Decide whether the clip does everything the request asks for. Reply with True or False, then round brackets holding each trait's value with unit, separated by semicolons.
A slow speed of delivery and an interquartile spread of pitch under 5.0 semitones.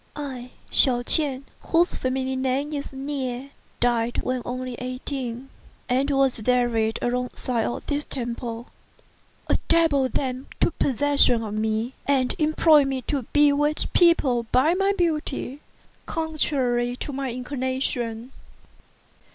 True (120 wpm; 2.8 semitones)